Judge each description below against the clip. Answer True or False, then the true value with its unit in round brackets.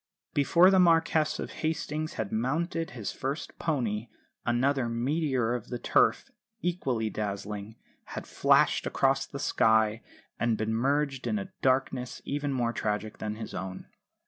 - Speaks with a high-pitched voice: False (125 Hz)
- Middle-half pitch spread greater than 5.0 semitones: True (5.4 semitones)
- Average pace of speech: True (145 wpm)